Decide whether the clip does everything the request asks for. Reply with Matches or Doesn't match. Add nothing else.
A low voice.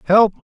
Doesn't match